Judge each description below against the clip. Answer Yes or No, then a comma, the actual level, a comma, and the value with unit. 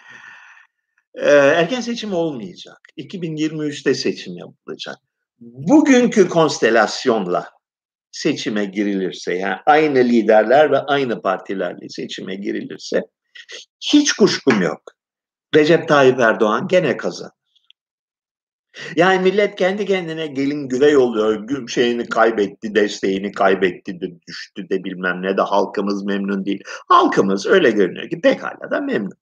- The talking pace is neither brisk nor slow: Yes, average, 110 wpm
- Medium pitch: Yes, medium, 155 Hz